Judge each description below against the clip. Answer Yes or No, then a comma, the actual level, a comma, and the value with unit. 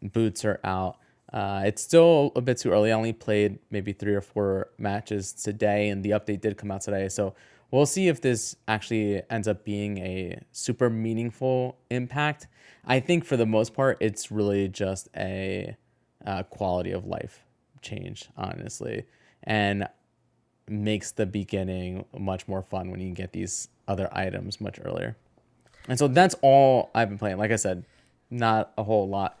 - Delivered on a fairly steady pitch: No, average, 3.1 semitones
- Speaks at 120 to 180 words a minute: Yes, average, 175 wpm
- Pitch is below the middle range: Yes, low, 105 Hz